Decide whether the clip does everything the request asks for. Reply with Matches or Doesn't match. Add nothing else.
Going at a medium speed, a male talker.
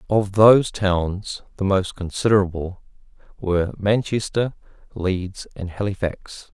Doesn't match